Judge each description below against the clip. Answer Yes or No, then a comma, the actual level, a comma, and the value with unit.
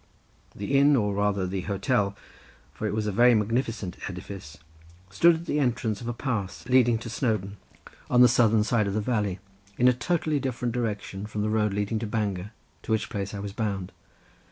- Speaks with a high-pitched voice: No, low, 110 Hz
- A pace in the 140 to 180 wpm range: No, average, 195 wpm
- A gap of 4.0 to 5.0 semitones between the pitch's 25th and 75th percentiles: No, average, 3.3 semitones